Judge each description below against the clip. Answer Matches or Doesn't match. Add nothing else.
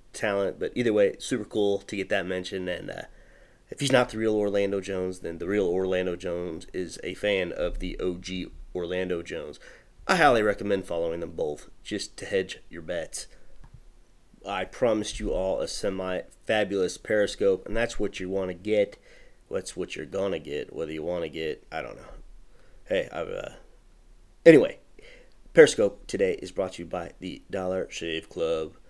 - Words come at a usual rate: Matches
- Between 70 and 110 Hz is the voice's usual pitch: Matches